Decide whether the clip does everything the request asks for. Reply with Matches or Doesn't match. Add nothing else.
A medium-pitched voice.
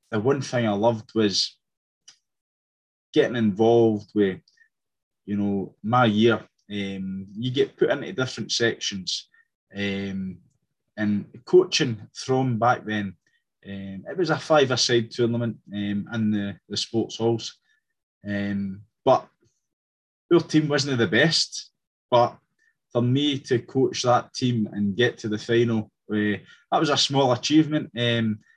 Doesn't match